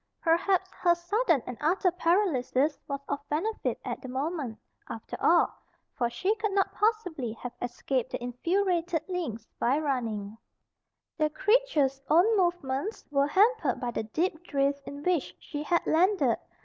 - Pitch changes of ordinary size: No, wide, 5.8 semitones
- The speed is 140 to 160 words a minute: Yes, average, 150 wpm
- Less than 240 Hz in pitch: No, very high, 315 Hz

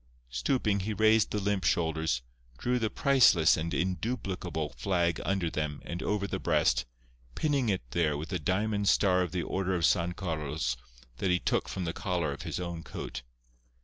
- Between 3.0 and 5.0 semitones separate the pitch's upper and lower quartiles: Yes, average, 4.1 semitones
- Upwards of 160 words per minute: Yes, average, 180 wpm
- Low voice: Yes, very low, 90 Hz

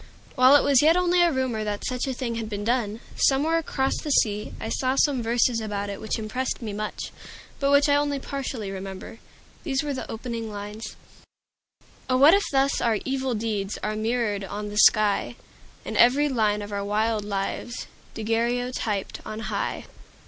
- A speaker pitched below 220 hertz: No, high, 230 Hz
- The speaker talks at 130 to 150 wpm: No, average, 180 wpm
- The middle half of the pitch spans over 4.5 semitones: No, average, 4.2 semitones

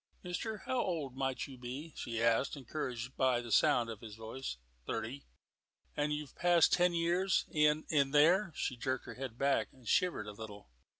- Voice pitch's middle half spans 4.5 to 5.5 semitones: Yes, average, 5.2 semitones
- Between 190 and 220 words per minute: No, average, 180 wpm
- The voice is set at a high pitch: No, low, 135 Hz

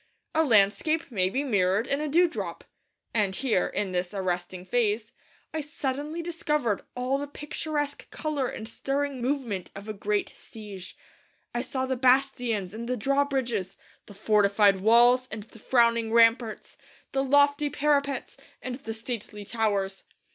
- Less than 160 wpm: Yes, average, 145 wpm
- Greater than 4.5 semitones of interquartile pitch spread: Yes, average, 5.2 semitones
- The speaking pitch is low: No, high, 235 Hz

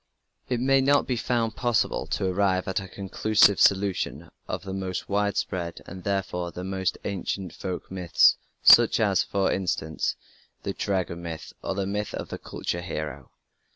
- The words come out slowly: No, average, 160 wpm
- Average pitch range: No, narrow, 2.3 semitones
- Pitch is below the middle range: Yes, very low, 95 Hz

